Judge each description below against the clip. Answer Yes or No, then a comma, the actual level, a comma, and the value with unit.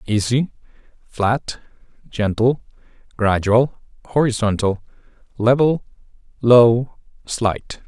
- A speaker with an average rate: No, slow, 60 wpm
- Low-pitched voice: Yes, low, 115 Hz